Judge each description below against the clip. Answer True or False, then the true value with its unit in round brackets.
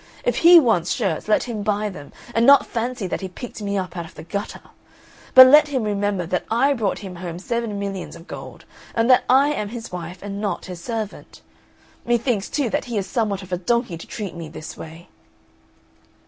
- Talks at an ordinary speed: False (210 wpm)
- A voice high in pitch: True (205 Hz)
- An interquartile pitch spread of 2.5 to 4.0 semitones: False (4.6 semitones)